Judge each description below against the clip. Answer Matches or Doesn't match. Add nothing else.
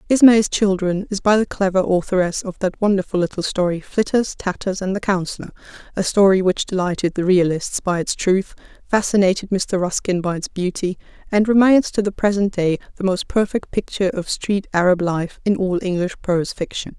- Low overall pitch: Doesn't match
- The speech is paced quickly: Doesn't match